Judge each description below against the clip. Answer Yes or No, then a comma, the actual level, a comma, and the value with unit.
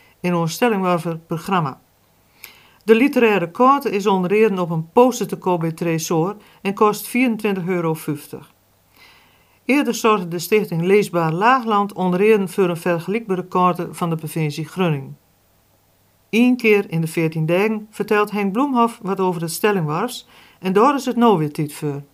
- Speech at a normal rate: Yes, average, 155 wpm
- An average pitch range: Yes, average, 4.6 semitones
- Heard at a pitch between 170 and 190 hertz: Yes, medium, 185 Hz